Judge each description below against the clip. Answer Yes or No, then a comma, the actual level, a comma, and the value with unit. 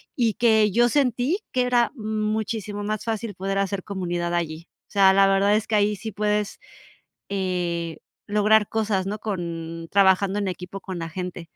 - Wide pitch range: No, average, 2.9 semitones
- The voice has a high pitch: Yes, high, 200 Hz